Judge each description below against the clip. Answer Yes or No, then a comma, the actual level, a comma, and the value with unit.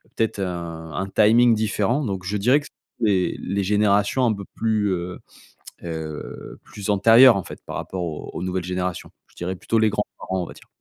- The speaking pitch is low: Yes, low, 100 Hz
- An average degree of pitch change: Yes, average, 3.1 semitones